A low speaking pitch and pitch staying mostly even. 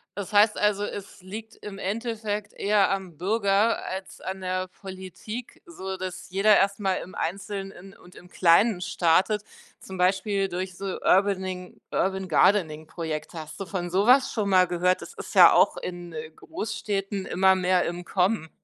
No: high, 190 Hz; narrow, 2.1 semitones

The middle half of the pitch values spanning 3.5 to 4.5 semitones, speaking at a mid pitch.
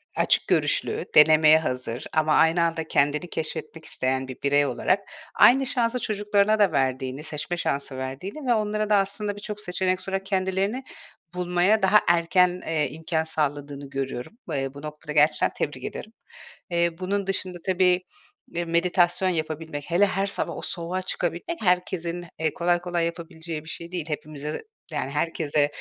Yes: average, 3.9 semitones; medium, 170 Hz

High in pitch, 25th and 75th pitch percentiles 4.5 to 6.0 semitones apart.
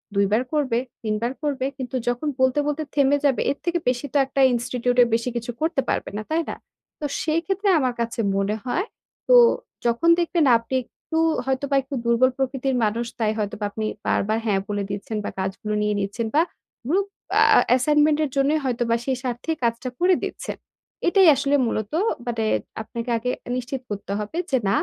No: very high, 250 Hz; average, 4.0 semitones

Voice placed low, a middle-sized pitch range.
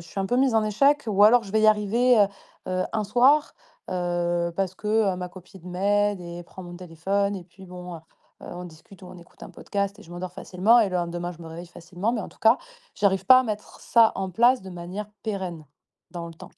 No: high, 190 Hz; average, 3.3 semitones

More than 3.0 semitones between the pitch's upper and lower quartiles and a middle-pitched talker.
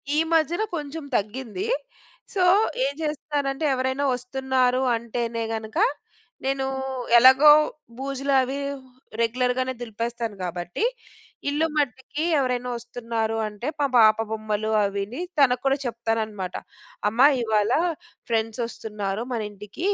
No: average, 3.7 semitones; high, 245 Hz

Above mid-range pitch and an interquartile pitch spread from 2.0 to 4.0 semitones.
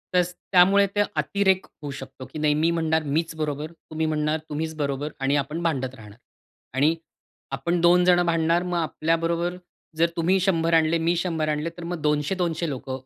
No: medium, 160 Hz; narrow, 2.4 semitones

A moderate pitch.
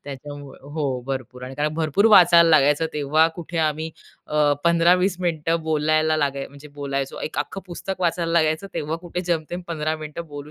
Yes: medium, 155 Hz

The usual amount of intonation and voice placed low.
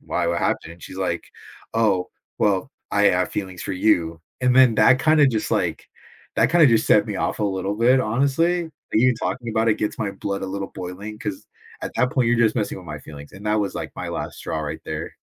Yes: average, 4.5 semitones; low, 105 Hz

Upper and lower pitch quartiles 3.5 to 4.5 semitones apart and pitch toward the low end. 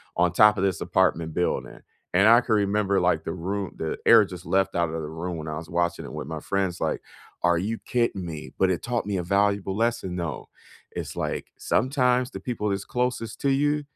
Yes: average, 4.1 semitones; very low, 95 Hz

